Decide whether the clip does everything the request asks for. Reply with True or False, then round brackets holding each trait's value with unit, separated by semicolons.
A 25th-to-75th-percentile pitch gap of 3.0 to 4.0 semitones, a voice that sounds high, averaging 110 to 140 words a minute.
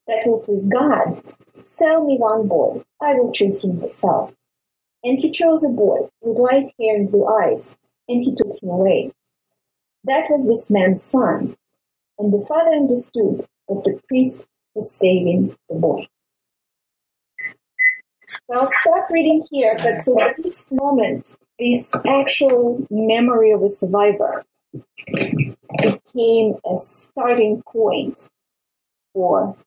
False (4.7 semitones; 240 Hz; 135 wpm)